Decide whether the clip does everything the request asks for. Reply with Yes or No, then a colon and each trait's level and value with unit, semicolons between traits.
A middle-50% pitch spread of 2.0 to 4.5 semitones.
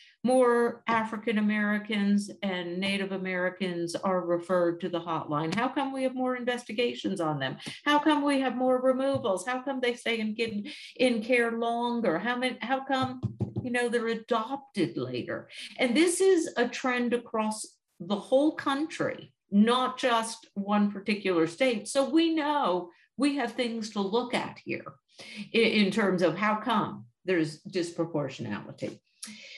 No: average, 5.0 semitones